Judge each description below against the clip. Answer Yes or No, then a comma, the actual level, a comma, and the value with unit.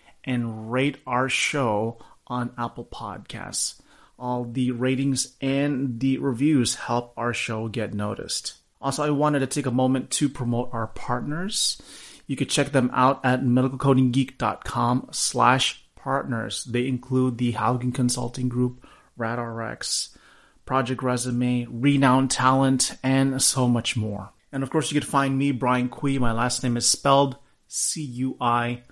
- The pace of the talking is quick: No, average, 140 wpm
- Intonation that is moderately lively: No, narrow, 2.0 semitones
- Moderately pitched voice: No, low, 125 Hz